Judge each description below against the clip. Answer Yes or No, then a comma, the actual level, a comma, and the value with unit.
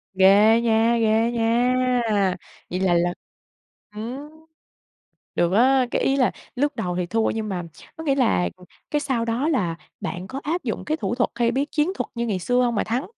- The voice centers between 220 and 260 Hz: Yes, high, 235 Hz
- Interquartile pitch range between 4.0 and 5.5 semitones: Yes, average, 4.4 semitones